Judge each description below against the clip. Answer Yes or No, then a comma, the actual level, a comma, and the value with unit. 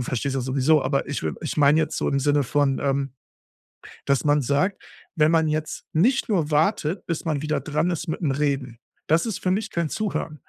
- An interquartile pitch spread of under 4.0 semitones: Yes, average, 2.8 semitones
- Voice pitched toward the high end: No, medium, 150 Hz